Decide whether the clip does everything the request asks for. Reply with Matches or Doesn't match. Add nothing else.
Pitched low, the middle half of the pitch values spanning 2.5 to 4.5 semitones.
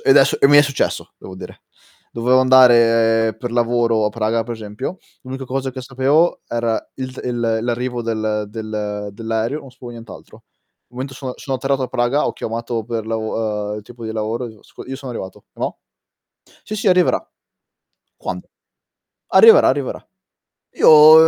Matches